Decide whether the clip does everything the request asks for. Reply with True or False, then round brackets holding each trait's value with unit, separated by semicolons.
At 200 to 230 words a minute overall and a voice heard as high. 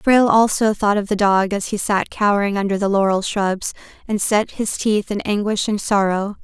True (205 wpm; 205 Hz)